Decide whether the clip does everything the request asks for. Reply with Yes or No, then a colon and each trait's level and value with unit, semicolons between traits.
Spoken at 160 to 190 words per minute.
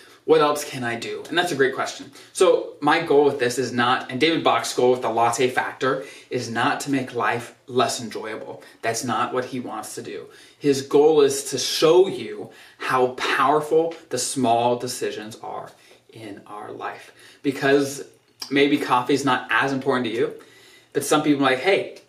Yes: average, 185 wpm